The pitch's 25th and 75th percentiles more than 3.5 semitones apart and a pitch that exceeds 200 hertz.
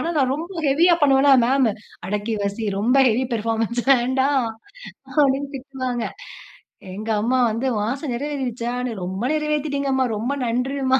No: average, 3.1 semitones; very high, 260 Hz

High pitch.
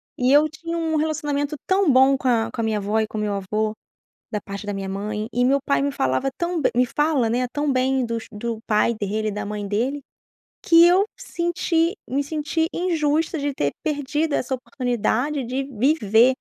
Yes: very high, 260 Hz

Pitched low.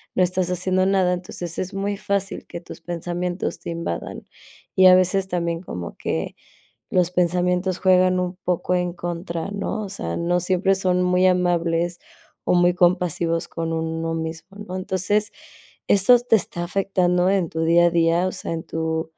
No: medium, 180 Hz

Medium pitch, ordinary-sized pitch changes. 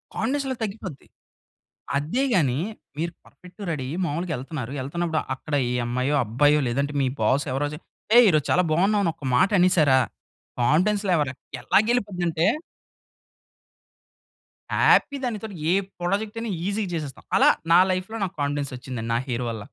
No: medium, 160 Hz; wide, 6.0 semitones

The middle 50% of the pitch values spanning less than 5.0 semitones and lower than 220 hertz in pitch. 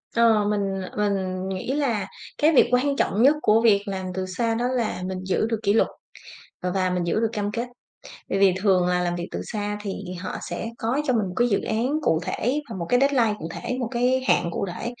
Yes: average, 4.3 semitones; high, 210 Hz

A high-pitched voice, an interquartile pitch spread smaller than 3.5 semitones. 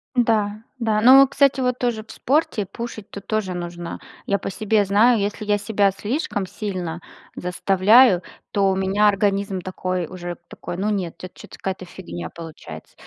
Yes: high, 200 Hz; average, 3.0 semitones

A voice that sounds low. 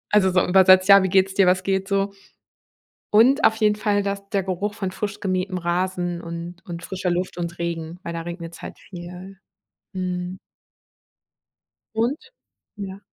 No: medium, 185 Hz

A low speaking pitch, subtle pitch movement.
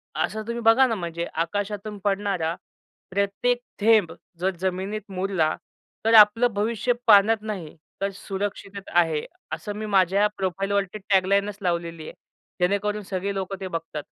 No: high, 200 Hz; narrow, 2.3 semitones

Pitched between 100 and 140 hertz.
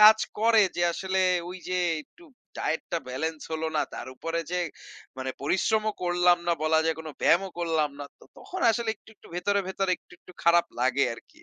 No: medium, 175 Hz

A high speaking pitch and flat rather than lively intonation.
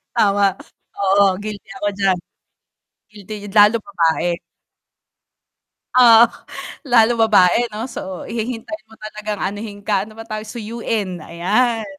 Yes: high, 215 Hz; narrow, 2.2 semitones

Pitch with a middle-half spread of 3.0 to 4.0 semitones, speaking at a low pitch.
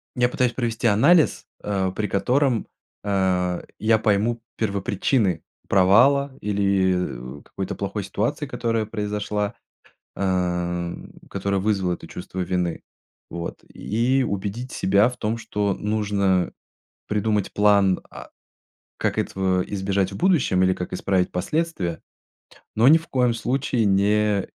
Yes: average, 3.5 semitones; low, 100 Hz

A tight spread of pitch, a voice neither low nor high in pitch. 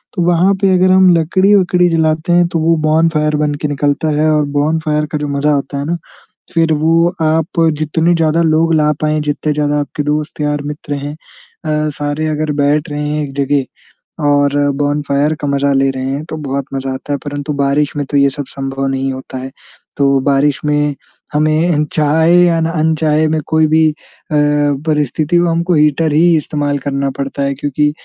Yes: narrow, 1.9 semitones; medium, 150 Hz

